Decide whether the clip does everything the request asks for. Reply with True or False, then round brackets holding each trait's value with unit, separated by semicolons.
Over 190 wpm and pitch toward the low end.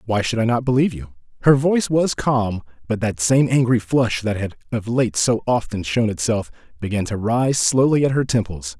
True (205 wpm; 115 Hz)